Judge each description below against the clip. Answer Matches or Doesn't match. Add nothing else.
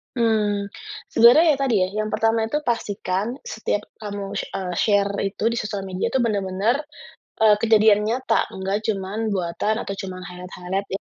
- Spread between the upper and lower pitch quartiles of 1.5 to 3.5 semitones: Matches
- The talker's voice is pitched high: Matches